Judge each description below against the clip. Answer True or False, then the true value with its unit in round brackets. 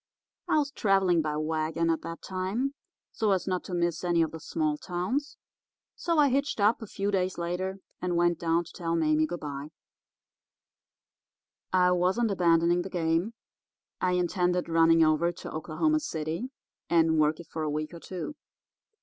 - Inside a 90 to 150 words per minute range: False (170 wpm)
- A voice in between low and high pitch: True (175 Hz)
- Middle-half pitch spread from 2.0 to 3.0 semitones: True (2.7 semitones)